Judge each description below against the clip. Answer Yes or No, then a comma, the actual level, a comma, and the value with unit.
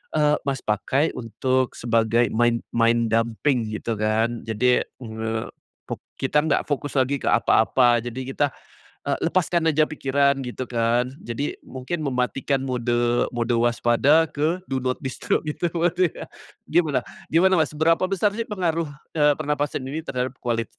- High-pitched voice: No, low, 130 Hz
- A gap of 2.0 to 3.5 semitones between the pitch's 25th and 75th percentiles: No, average, 4.4 semitones